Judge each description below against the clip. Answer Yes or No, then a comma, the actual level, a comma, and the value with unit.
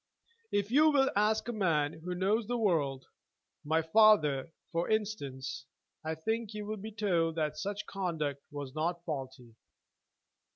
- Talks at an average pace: Yes, average, 150 wpm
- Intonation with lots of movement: Yes, wide, 6.1 semitones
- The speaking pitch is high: No, medium, 170 Hz